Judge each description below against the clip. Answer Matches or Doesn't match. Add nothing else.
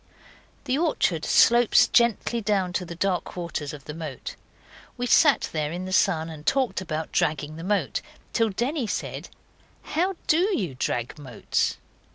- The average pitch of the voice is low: Doesn't match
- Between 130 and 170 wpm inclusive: Matches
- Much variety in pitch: Matches